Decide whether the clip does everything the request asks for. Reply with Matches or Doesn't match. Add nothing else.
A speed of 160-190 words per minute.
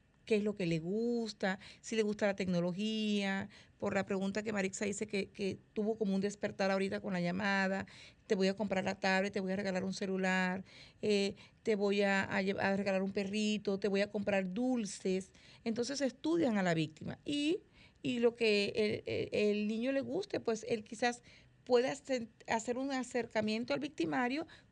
Matches